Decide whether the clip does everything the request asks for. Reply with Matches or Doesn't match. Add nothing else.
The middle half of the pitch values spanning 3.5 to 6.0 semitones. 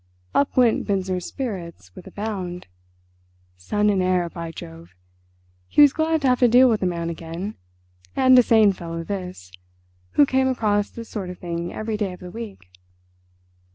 Matches